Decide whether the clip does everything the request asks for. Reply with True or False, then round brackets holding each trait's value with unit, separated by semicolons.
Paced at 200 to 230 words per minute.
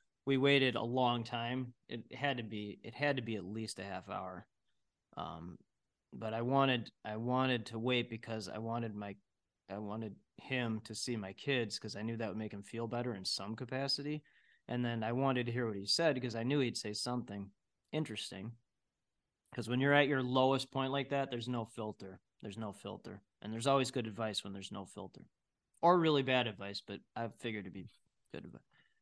True (205 wpm)